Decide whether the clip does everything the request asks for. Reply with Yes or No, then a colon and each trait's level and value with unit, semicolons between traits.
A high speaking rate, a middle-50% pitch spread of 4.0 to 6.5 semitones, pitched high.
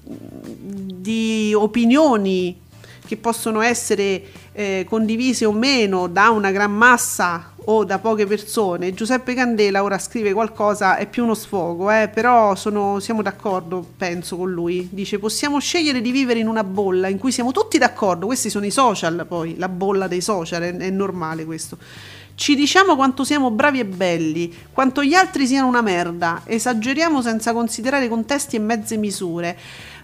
No: average, 160 wpm; average, 4.4 semitones; high, 215 Hz